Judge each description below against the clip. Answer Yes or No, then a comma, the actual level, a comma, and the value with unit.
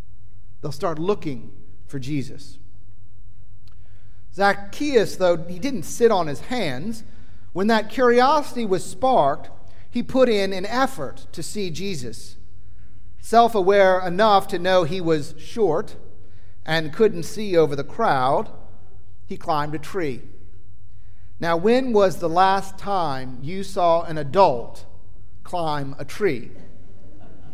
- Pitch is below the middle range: No, medium, 150 Hz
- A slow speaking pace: Yes, slow, 125 wpm